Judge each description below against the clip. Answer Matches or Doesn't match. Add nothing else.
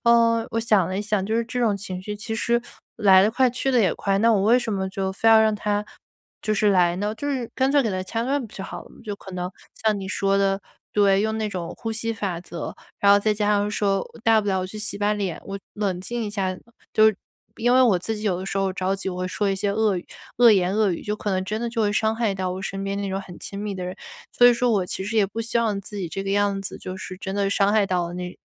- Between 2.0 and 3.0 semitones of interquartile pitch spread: Matches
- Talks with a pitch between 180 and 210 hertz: Matches